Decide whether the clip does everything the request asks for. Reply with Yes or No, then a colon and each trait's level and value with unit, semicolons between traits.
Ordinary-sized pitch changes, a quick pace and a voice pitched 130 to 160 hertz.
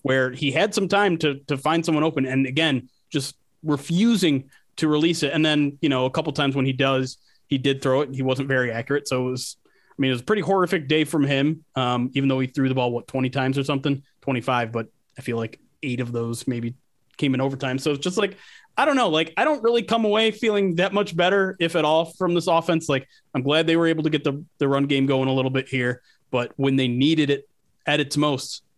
Yes: average, 3.5 semitones; fast, 255 wpm; medium, 140 Hz